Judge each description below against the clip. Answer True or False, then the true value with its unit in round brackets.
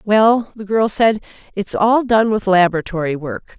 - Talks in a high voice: True (205 Hz)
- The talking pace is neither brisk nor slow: True (165 wpm)